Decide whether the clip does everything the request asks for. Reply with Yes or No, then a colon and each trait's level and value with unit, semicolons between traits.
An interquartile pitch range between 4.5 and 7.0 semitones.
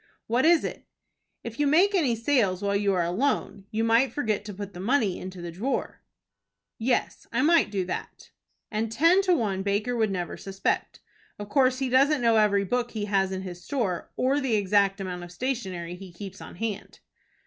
Yes: average, 5.1 semitones